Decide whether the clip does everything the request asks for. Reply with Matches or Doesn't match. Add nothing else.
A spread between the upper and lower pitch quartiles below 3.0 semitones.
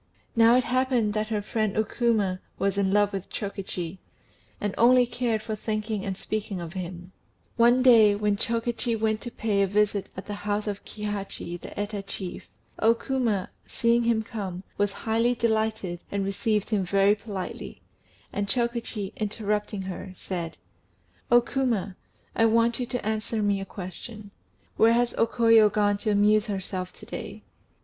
Matches